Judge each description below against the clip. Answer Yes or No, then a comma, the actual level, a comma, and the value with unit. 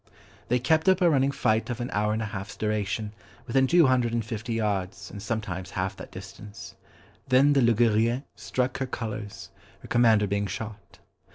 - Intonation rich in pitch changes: No, average, 3.4 semitones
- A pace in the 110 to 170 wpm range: No, average, 180 wpm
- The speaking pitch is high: No, low, 110 Hz